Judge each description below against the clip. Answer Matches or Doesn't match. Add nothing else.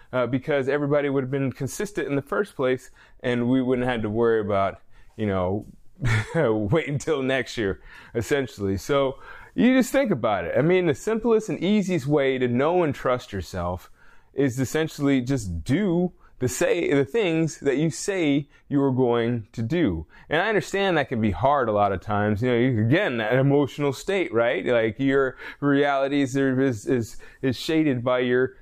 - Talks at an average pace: Matches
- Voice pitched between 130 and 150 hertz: Matches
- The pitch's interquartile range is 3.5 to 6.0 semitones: Matches